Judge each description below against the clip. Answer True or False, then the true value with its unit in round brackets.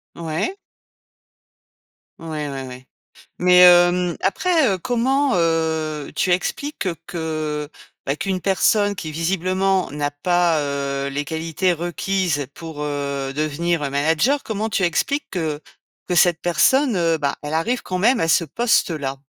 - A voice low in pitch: False (170 Hz)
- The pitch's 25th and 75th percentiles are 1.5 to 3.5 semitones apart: False (4.0 semitones)